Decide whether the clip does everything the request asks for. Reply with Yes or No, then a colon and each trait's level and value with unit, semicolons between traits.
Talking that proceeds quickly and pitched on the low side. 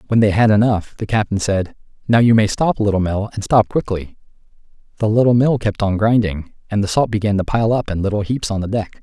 Yes: fast, 235 wpm; low, 105 Hz